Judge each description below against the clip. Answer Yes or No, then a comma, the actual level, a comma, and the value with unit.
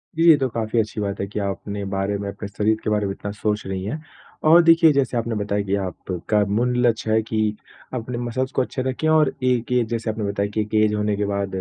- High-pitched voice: No, low, 110 Hz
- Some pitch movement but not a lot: Yes, average, 3.3 semitones